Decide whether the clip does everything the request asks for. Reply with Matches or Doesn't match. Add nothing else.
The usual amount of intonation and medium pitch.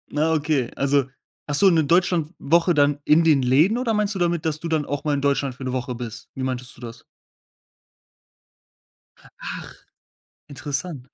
Matches